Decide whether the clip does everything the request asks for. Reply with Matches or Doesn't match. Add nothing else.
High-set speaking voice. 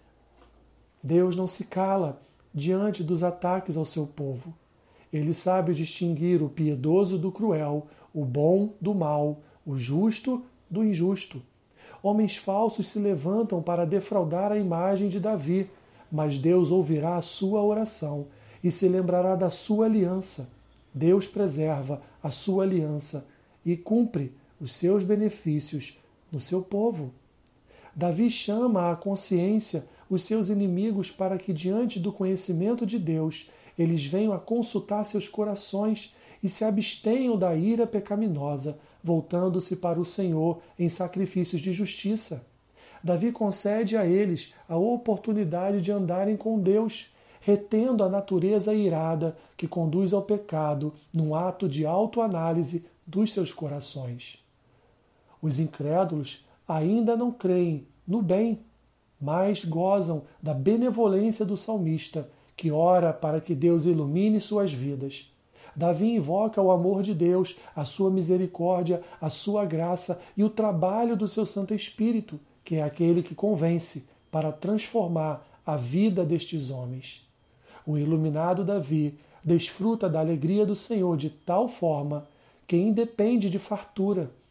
Doesn't match